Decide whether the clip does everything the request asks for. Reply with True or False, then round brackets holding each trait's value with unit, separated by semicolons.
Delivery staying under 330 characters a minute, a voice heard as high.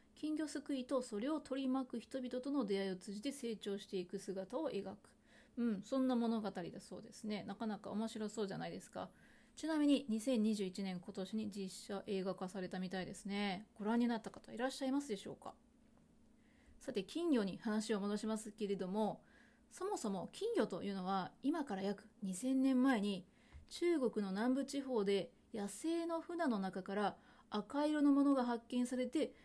False (335 characters per minute; 220 Hz)